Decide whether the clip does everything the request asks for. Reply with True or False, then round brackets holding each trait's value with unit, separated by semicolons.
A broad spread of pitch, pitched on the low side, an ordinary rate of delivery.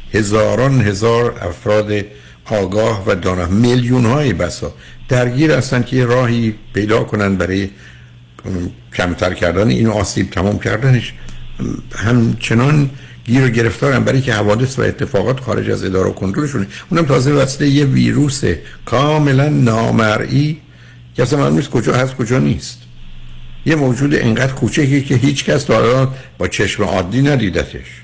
True (5.7 semitones; 115 Hz; 135 wpm)